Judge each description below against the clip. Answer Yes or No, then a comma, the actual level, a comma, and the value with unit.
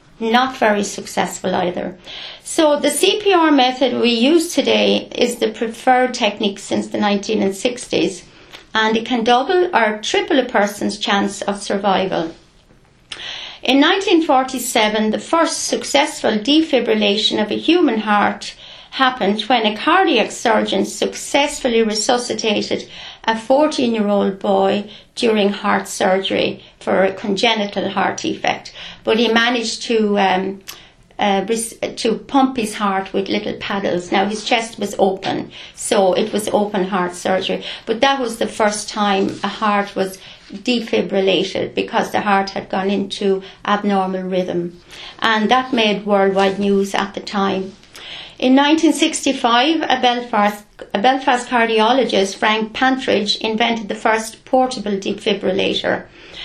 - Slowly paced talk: Yes, slow, 130 wpm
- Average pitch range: Yes, average, 4.2 semitones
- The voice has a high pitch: Yes, high, 220 Hz